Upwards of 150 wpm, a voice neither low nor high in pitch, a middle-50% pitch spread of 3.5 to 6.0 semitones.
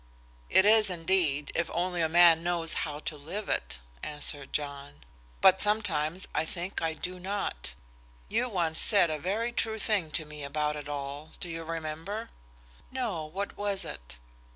Yes: average, 165 wpm; medium, 165 Hz; average, 4.4 semitones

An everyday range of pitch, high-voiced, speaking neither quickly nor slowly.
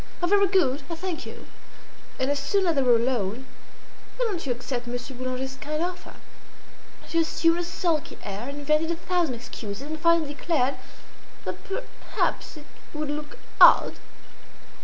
Yes: average, 4.7 semitones; very high, 295 Hz; average, 160 wpm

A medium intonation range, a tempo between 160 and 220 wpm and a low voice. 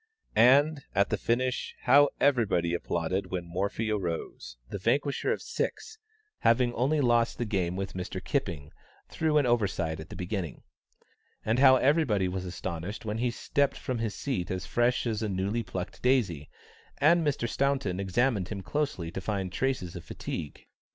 No: wide, 6.1 semitones; average, 165 wpm; low, 110 Hz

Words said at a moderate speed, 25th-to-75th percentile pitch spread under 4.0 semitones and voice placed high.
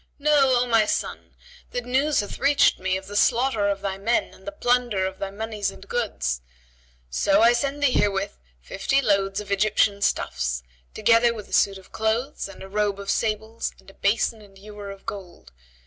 Yes: average, 195 wpm; average, 3.5 semitones; high, 210 Hz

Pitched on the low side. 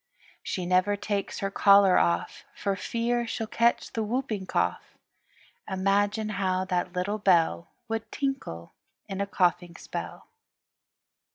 No: high, 200 Hz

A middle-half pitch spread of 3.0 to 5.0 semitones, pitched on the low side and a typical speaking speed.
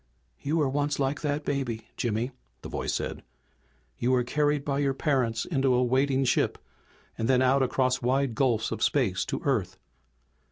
No: narrow, 2.5 semitones; low, 130 Hz; average, 170 wpm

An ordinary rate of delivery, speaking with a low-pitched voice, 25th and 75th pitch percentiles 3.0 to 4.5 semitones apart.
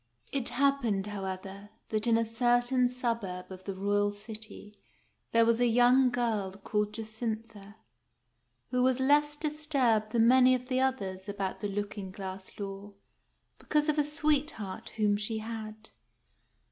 No: average, 145 wpm; high, 220 Hz; average, 3.6 semitones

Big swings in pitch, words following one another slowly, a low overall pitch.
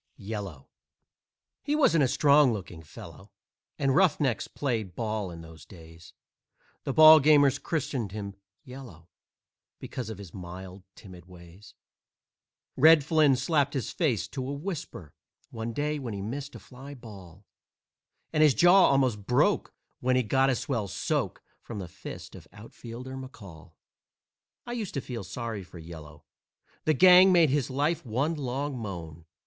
No: wide, 6.9 semitones; average, 150 wpm; low, 125 Hz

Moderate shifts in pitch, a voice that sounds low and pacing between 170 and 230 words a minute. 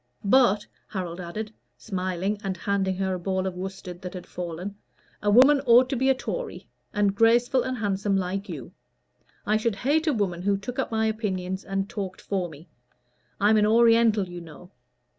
No: average, 3.4 semitones; high, 200 Hz; average, 180 wpm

